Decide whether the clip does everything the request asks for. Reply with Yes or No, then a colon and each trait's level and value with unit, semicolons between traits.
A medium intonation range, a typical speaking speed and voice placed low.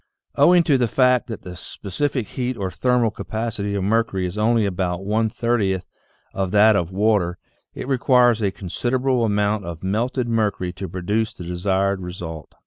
Yes: average, 4.0 semitones; average, 170 wpm; low, 105 Hz